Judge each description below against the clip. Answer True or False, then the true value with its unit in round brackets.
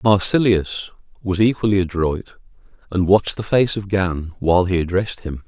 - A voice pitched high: False (95 Hz)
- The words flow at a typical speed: True (155 wpm)